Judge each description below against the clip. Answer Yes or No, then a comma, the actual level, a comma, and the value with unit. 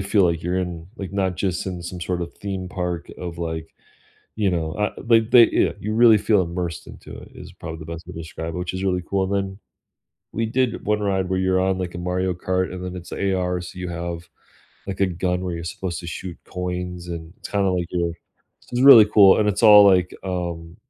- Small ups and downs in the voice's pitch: Yes, narrow, 2.0 semitones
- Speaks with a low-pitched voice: Yes, very low, 90 Hz